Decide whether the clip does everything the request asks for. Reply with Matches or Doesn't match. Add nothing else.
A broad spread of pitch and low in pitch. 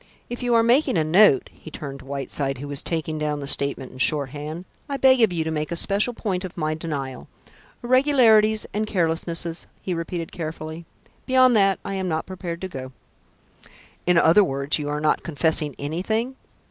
Doesn't match